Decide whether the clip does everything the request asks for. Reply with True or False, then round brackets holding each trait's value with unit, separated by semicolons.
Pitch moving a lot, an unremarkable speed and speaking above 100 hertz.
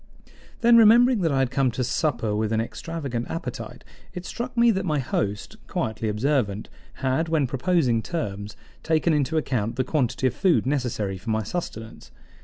True (6.7 semitones; 170 wpm; 135 Hz)